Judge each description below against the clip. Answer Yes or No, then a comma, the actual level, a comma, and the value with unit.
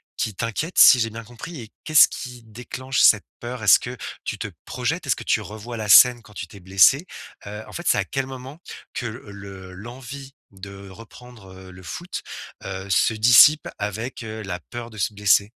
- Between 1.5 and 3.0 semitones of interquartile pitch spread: No, average, 3.8 semitones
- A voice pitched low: Yes, low, 110 Hz